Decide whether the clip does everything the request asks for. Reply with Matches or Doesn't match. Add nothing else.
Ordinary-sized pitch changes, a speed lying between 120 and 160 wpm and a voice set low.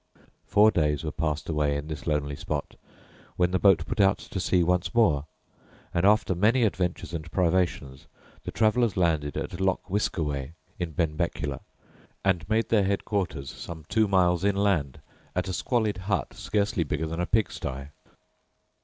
Matches